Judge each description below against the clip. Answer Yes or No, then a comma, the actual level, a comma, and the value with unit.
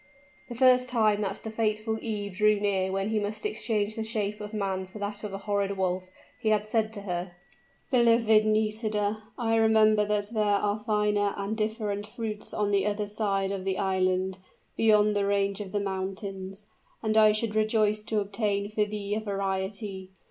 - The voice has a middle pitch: No, high, 210 Hz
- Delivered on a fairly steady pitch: Yes, narrow, 1.5 semitones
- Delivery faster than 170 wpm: Yes, average, 180 wpm